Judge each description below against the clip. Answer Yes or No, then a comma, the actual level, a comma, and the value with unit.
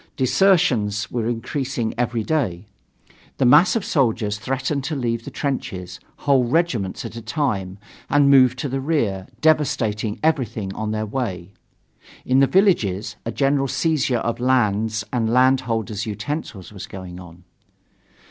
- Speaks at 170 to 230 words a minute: No, average, 140 wpm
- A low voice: Yes, low, 120 Hz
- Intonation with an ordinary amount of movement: Yes, average, 4.5 semitones